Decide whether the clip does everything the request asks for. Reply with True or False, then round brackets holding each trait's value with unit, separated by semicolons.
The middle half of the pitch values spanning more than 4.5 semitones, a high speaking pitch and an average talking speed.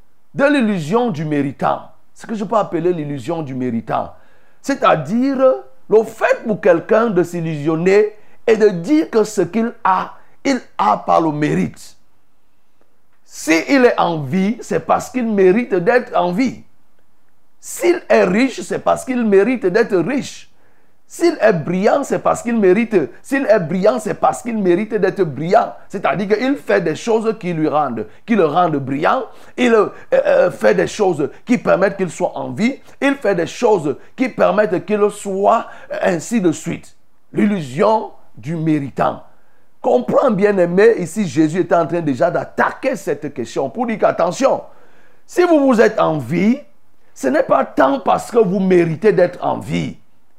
True (5.5 semitones; 210 Hz; 165 wpm)